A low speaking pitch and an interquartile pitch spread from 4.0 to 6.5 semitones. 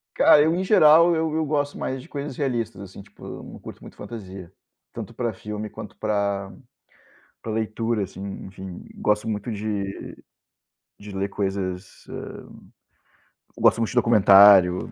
Yes: low, 105 Hz; average, 4.3 semitones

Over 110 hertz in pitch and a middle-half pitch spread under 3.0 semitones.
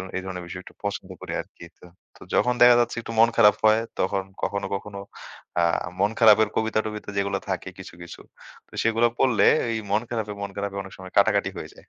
No: low, 105 Hz; narrow, 2.4 semitones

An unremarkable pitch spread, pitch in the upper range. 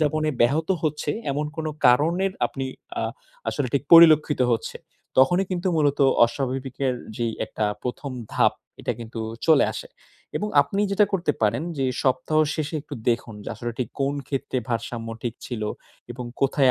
No: average, 4.2 semitones; medium, 140 Hz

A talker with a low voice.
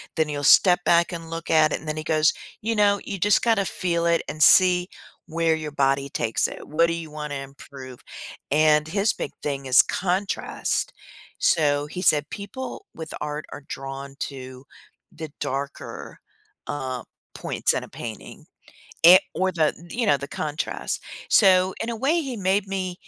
No: medium, 160 Hz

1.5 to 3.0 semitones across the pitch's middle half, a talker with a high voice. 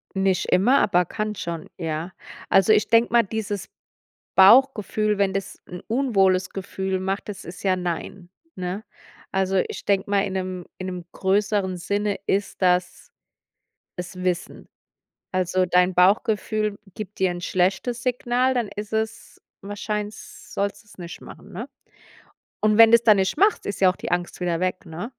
Yes: narrow, 2.6 semitones; high, 195 Hz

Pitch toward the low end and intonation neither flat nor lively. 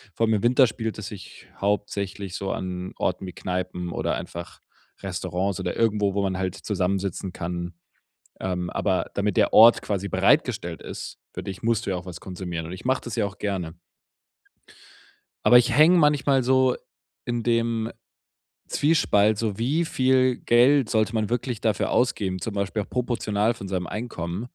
Yes: low, 105 Hz; average, 4.3 semitones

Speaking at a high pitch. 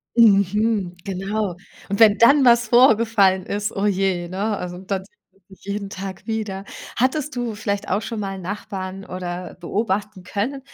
Yes: high, 200 Hz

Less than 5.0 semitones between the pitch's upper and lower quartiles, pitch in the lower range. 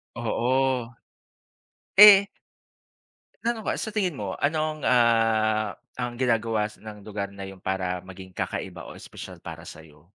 No: average, 5.3 semitones; low, 115 Hz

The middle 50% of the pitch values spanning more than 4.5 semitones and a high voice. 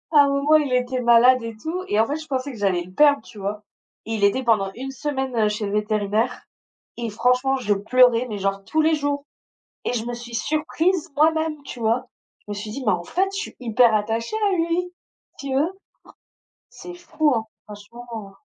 Yes: average, 5.3 semitones; high, 245 Hz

